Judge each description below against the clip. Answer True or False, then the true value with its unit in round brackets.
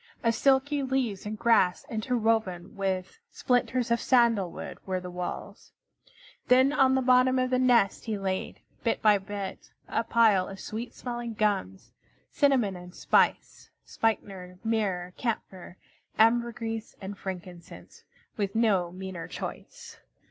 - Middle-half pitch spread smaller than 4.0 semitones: False (4.3 semitones)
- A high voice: True (220 Hz)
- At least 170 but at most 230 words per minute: False (135 wpm)